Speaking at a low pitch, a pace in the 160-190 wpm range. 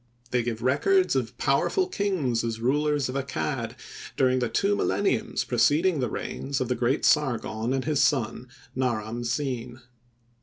No: low, 130 Hz; average, 150 wpm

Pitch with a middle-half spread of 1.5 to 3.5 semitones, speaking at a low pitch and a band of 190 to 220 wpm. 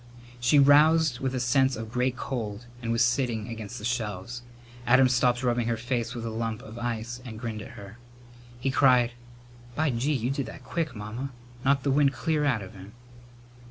Yes: average, 2.8 semitones; low, 120 Hz; average, 195 wpm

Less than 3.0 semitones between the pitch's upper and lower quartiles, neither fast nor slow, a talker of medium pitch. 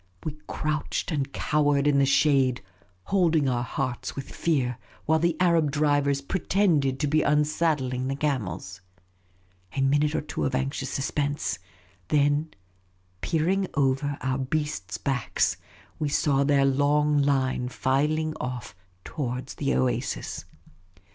No: narrow, 2.4 semitones; slow, 130 wpm; medium, 145 Hz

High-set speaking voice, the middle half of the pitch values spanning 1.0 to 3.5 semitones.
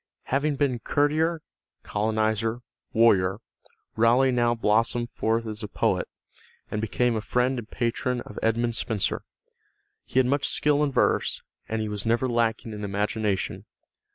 No: low, 115 Hz; narrow, 2.6 semitones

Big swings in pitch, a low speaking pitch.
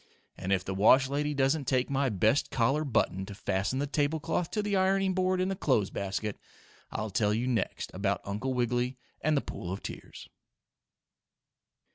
Yes: wide, 6.5 semitones; low, 130 Hz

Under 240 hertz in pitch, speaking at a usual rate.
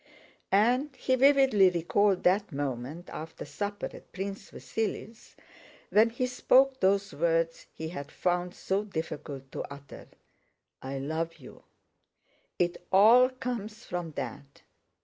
No: high, 190 Hz; slow, 125 wpm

